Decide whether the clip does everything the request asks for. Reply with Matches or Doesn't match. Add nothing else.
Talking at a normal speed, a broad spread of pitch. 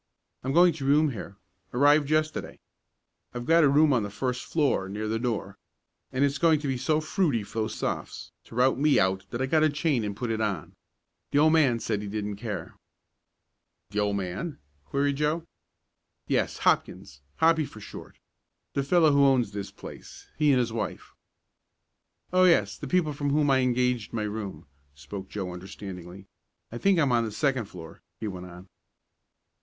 Matches